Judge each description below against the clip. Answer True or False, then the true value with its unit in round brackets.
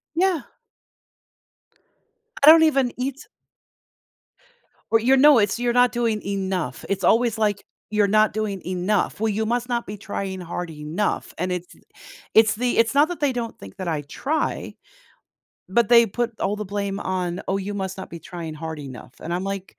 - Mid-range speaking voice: False (205 Hz)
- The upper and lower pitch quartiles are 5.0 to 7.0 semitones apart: False (4.4 semitones)